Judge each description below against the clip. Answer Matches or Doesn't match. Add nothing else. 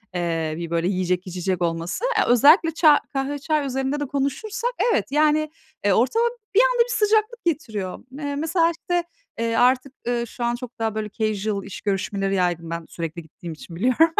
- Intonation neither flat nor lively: Doesn't match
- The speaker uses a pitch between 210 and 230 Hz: Doesn't match